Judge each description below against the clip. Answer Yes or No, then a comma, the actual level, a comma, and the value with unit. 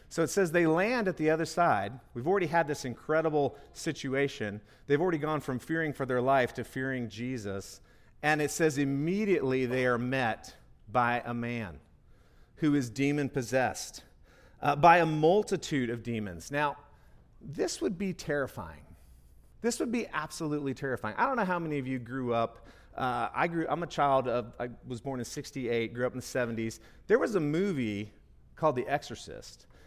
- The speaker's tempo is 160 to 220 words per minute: Yes, average, 175 wpm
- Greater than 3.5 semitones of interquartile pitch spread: Yes, average, 4.7 semitones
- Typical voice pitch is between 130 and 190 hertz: Yes, low, 135 Hz